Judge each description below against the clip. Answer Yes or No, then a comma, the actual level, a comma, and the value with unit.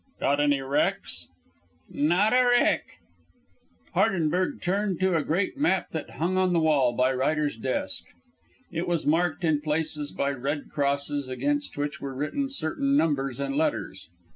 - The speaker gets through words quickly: No, average, 150 wpm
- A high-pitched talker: No, medium, 155 Hz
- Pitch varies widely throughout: No, average, 4.5 semitones